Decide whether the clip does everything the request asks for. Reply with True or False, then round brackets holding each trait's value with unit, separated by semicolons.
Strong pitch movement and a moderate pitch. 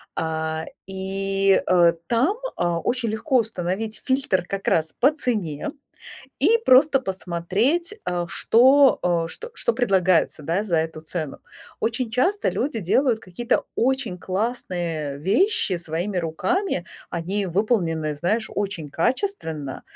False (6.5 semitones; 195 Hz)